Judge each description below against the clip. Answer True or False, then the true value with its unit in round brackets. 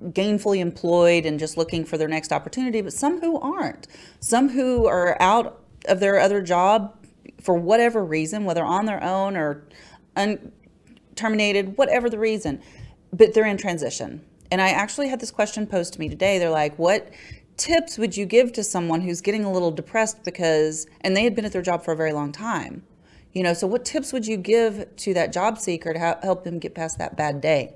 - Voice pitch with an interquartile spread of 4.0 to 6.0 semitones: True (4.5 semitones)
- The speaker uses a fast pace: True (210 wpm)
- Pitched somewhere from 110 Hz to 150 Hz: False (195 Hz)